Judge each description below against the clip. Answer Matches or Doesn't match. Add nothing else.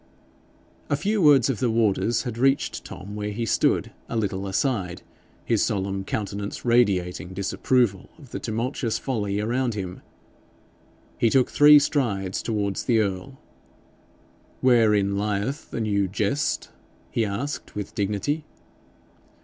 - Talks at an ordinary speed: Doesn't match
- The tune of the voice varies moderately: Matches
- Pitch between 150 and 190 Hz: Doesn't match